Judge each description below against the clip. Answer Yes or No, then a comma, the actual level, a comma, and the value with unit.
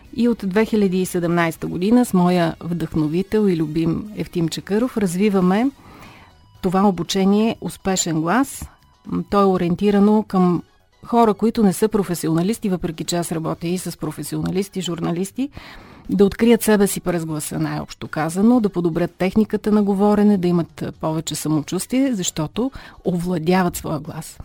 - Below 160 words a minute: Yes, average, 135 wpm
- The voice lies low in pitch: No, medium, 180 Hz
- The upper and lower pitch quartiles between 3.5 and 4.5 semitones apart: Yes, average, 4.0 semitones